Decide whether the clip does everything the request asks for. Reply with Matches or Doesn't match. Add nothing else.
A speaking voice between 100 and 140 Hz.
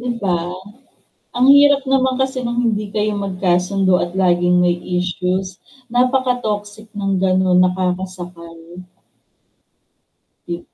Doesn't match